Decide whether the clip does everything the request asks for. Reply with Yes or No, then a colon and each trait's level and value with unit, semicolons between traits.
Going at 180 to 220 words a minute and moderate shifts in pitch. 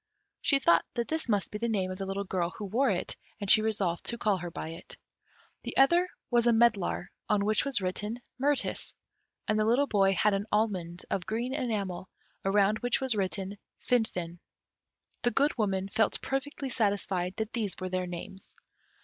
Yes: average, 185 wpm; average, 3.9 semitones